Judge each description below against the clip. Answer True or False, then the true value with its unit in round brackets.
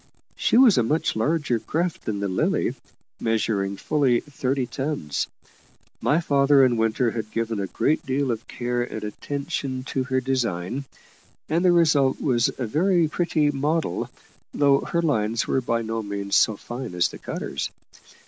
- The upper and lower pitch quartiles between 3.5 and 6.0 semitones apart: True (4.6 semitones)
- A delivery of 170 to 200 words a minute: False (160 wpm)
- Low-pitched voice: True (130 Hz)